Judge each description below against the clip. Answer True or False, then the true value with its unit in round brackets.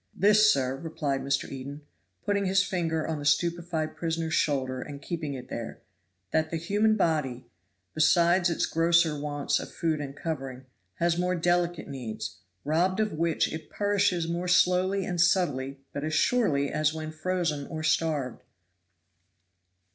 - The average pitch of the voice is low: False (160 Hz)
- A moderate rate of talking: True (155 wpm)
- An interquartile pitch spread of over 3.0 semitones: True (3.6 semitones)